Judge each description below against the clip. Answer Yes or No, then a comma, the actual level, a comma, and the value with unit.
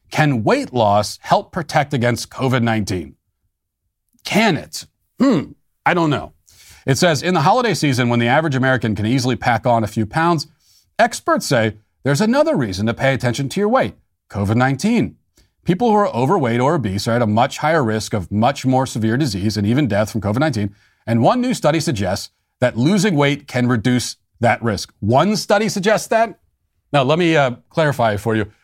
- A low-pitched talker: Yes, low, 125 Hz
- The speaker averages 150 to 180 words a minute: No, average, 190 wpm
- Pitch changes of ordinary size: No, wide, 6.3 semitones